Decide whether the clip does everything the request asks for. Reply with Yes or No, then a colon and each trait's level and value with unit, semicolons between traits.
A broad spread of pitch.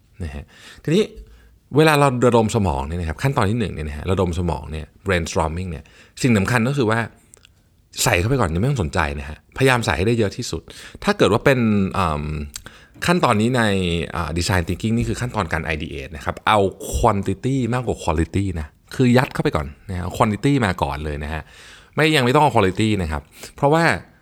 Yes: wide, 6.6 semitones